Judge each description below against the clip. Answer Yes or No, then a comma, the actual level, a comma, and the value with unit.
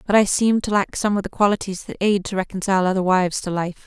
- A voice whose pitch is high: Yes, high, 195 Hz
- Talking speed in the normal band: No, fast, 265 wpm